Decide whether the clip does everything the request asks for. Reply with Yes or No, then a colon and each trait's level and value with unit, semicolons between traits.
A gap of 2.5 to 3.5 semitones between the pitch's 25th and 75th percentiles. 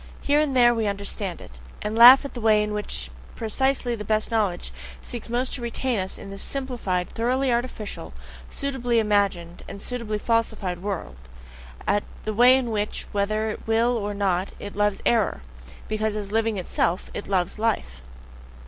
Yes: average, 3.0 semitones